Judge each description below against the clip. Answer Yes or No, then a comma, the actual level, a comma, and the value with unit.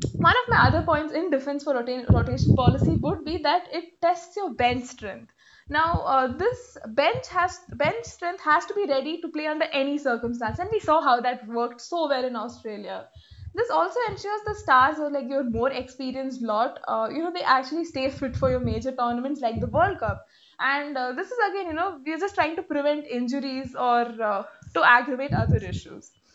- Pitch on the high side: Yes, very high, 285 Hz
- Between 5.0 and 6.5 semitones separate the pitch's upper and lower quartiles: Yes, average, 5.3 semitones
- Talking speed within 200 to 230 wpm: Yes, fast, 205 wpm